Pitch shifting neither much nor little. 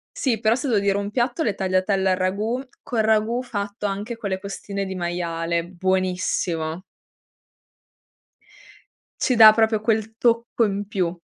Yes: average, 3.0 semitones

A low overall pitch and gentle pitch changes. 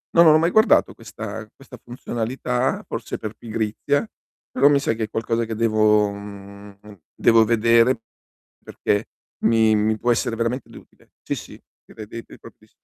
Yes: low, 115 Hz; narrow, 2.2 semitones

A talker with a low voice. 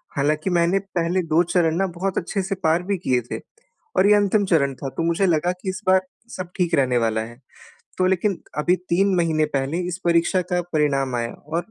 No: medium, 170 Hz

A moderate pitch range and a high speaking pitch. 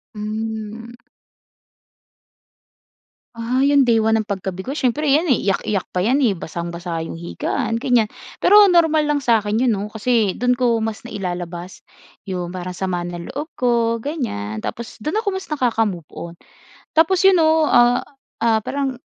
No: wide, 6.1 semitones; high, 230 Hz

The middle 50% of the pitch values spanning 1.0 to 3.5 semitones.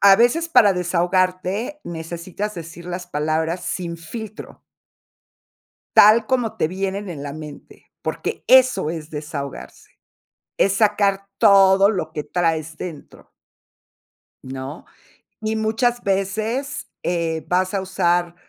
No: average, 4.1 semitones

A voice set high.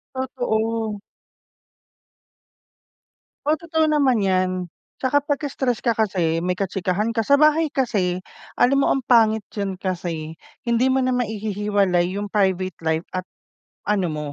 Yes: high, 215 Hz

